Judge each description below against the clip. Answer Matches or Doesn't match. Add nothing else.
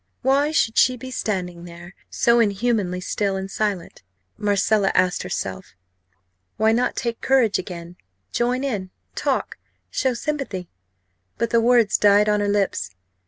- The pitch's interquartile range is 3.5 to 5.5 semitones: Matches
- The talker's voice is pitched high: Matches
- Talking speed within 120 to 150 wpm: Matches